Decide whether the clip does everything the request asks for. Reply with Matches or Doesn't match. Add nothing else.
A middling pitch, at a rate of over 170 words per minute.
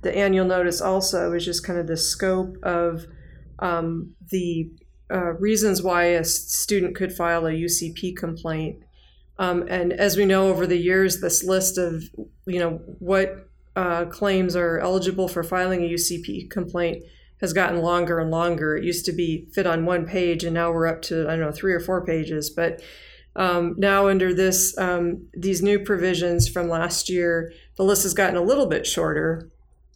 Matches